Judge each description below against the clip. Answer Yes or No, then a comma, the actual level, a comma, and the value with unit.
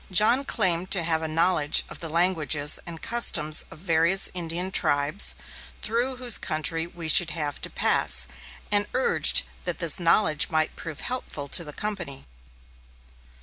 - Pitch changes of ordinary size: Yes, average, 3.5 semitones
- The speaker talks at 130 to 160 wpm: Yes, average, 150 wpm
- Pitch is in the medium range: Yes, medium, 170 Hz